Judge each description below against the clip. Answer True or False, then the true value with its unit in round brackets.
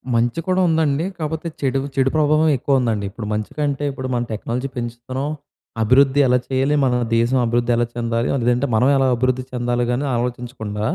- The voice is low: True (125 Hz)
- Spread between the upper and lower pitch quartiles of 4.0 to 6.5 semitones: False (2.6 semitones)